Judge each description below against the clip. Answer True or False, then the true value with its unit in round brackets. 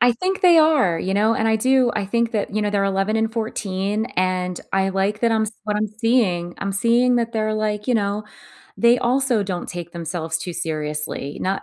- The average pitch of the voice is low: False (210 Hz)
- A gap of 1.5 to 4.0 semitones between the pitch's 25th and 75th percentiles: True (3.7 semitones)